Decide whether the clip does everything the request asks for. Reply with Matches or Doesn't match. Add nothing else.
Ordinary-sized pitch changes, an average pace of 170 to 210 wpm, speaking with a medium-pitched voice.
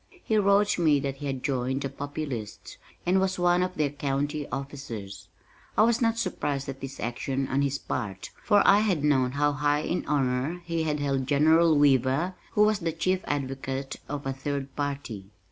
Matches